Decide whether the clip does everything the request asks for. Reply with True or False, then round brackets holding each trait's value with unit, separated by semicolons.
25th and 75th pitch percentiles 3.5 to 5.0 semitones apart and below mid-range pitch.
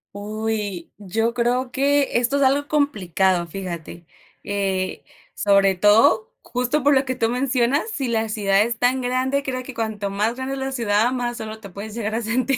False (4.1 semitones; 230 Hz)